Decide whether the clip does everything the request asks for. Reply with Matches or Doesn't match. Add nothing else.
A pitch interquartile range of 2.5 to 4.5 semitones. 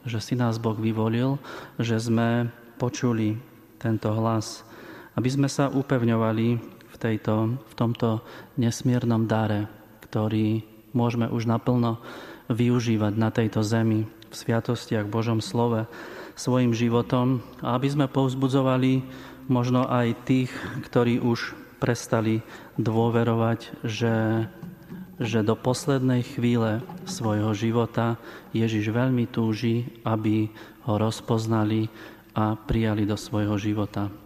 Doesn't match